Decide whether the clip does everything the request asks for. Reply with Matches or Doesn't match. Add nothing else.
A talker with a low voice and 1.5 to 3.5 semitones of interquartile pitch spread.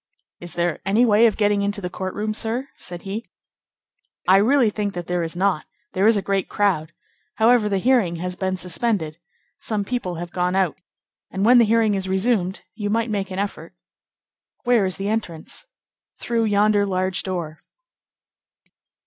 Doesn't match